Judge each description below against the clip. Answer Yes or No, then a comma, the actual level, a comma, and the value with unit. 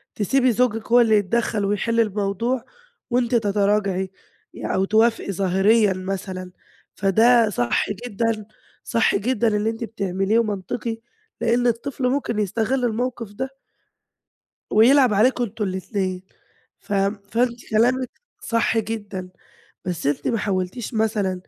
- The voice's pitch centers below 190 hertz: No, high, 220 Hz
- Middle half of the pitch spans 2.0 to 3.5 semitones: Yes, average, 3.2 semitones